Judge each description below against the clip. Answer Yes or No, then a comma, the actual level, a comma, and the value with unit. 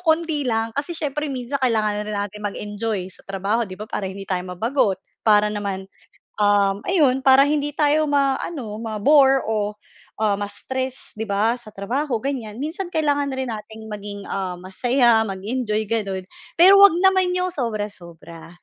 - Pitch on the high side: Yes, high, 225 Hz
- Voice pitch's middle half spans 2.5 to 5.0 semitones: No, wide, 5.5 semitones